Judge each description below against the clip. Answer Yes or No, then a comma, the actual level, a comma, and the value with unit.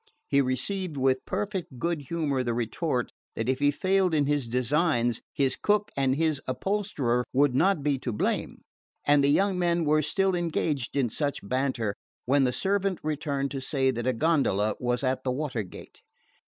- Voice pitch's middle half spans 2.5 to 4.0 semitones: No, average, 4.6 semitones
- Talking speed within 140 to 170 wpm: No, average, 180 wpm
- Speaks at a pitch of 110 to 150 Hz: Yes, medium, 140 Hz